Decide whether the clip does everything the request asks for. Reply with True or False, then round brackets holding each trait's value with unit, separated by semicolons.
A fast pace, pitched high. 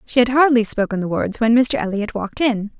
True (235 wpm; 230 Hz)